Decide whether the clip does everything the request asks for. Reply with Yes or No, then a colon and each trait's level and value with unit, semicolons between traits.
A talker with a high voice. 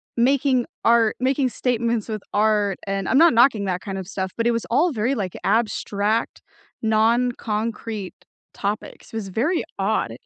Yes: high, 225 Hz